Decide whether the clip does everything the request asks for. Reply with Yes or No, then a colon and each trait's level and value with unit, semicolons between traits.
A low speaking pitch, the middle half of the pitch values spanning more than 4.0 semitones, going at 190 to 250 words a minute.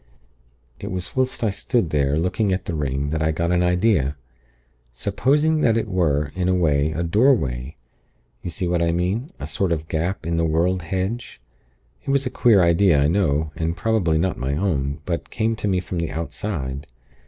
Yes: very low, 85 Hz; average, 4.5 semitones; average, 200 wpm